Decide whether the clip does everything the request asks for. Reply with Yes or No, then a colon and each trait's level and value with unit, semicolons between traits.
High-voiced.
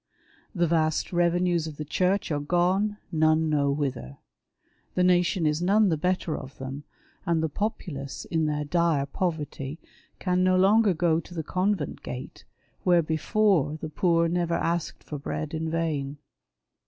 No: medium, 165 Hz